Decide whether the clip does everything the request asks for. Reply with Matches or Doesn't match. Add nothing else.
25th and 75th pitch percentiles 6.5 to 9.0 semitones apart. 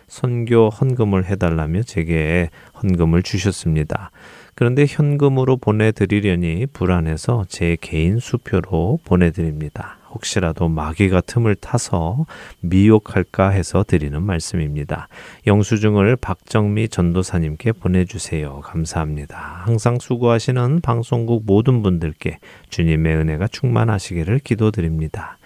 Doesn't match